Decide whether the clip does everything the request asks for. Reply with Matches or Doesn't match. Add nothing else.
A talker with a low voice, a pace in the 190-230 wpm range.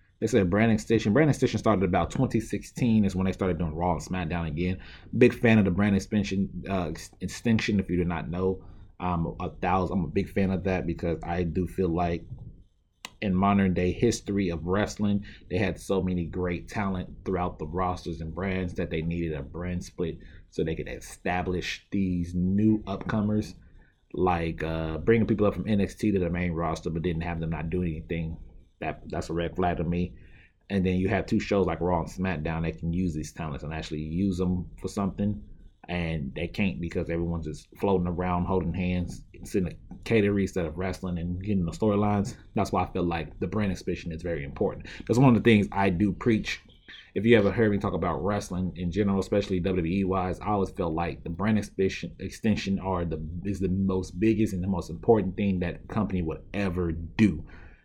Matches